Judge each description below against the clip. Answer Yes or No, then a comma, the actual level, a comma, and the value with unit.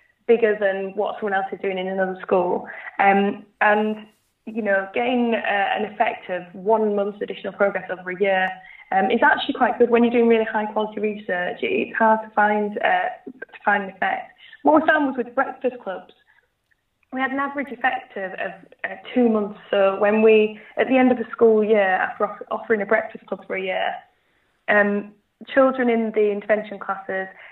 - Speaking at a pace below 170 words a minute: No, average, 190 wpm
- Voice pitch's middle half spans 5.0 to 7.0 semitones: No, average, 3.2 semitones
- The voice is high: Yes, high, 215 Hz